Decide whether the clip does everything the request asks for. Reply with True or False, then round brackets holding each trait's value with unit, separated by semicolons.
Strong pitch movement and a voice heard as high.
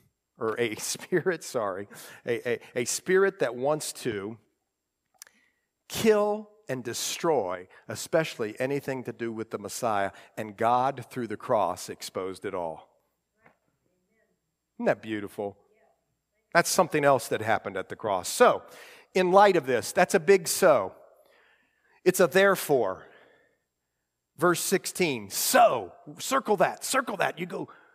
False (8.7 semitones; 150 Hz)